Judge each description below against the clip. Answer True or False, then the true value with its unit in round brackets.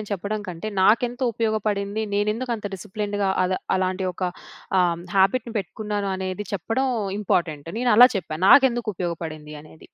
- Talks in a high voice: True (205 Hz)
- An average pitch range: True (3.0 semitones)